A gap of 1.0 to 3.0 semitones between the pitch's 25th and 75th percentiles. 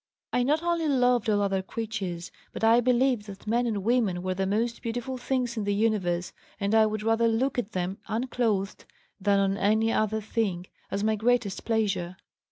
No: average, 3.4 semitones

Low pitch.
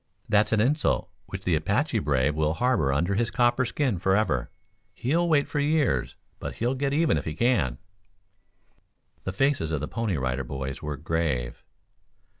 Yes: very low, 95 Hz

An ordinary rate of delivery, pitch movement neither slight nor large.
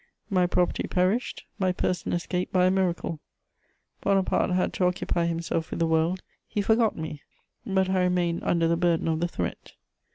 No: average, 170 wpm; narrow, 1.9 semitones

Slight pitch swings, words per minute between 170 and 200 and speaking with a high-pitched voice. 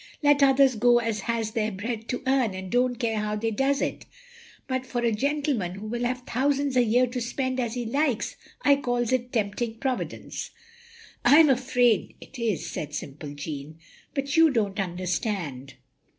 No: average, 3.9 semitones; average, 195 wpm; high, 240 Hz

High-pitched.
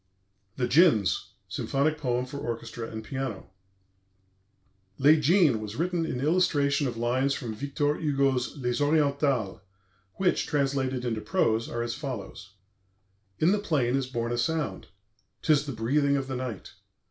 No: low, 135 Hz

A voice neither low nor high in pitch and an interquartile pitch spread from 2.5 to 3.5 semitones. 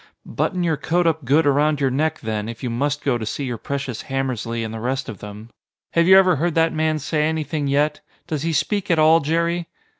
No: medium, 145 Hz; average, 4.2 semitones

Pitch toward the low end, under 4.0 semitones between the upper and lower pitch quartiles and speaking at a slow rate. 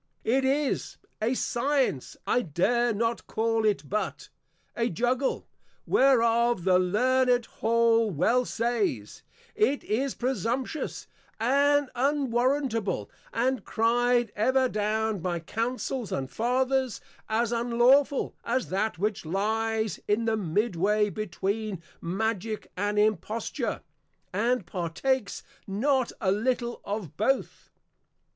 No: high, 230 Hz; average, 3.3 semitones; slow, 110 wpm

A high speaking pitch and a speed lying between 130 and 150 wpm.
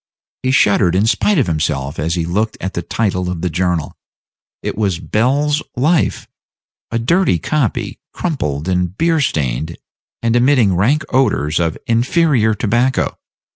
No: low, 105 Hz; average, 145 wpm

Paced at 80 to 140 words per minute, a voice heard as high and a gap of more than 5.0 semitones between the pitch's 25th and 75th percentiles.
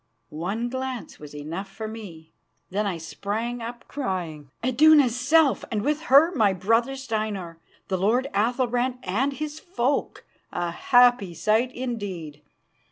Yes: slow, 135 wpm; high, 225 Hz; wide, 5.4 semitones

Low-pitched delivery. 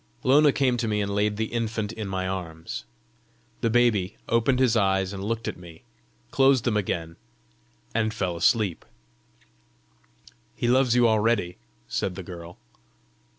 Yes: low, 105 Hz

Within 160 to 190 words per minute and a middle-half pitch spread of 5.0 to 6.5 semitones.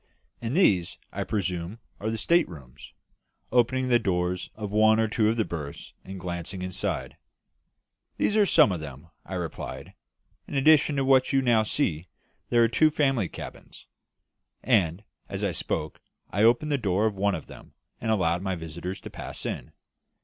Yes: average, 175 wpm; wide, 5.6 semitones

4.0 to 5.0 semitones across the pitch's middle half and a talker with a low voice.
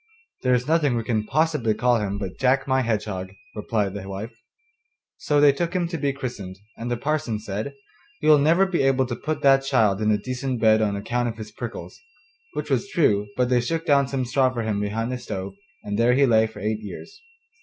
Yes: average, 4.5 semitones; low, 120 Hz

